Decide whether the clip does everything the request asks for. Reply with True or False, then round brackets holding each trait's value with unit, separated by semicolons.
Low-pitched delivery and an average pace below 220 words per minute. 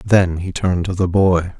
False (90 Hz; 225 wpm)